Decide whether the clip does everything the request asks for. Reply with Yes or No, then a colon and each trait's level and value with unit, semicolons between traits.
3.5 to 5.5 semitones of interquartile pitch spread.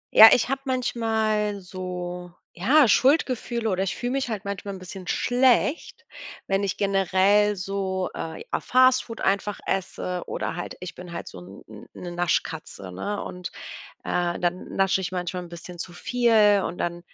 Yes: average, 3.8 semitones